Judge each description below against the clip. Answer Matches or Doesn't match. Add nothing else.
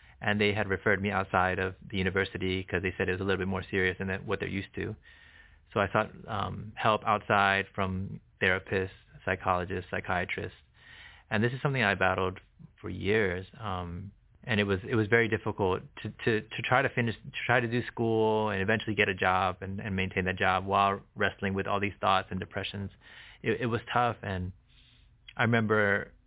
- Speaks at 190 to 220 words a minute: Matches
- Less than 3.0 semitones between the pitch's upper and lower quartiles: Matches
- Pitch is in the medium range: Doesn't match